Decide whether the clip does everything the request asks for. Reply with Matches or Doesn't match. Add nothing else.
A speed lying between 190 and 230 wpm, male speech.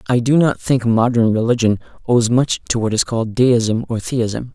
Matches